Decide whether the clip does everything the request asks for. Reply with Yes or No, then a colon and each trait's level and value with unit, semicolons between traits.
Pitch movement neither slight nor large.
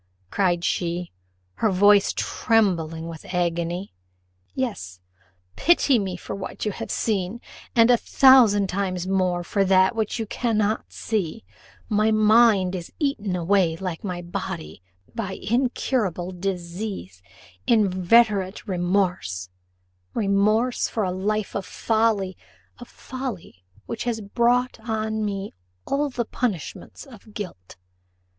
Yes: average, 3.8 semitones